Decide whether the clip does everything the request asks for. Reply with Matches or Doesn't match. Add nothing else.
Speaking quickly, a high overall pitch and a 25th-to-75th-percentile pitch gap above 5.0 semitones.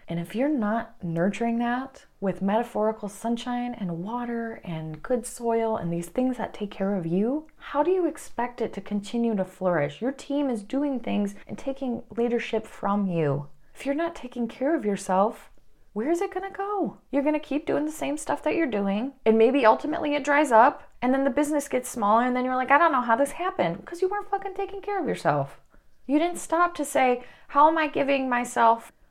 Matches